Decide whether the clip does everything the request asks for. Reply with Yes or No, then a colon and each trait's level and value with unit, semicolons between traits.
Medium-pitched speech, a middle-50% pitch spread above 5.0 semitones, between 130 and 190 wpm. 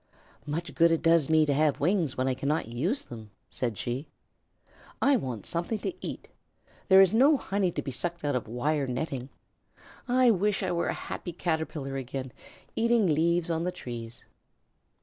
Yes: medium, 160 Hz; wide, 5.4 semitones; average, 175 wpm